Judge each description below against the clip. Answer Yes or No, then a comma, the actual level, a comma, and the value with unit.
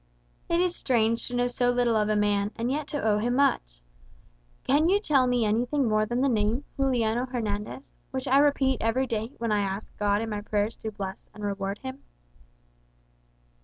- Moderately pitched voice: No, high, 230 Hz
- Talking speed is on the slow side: No, average, 200 wpm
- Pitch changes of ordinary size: Yes, average, 3.9 semitones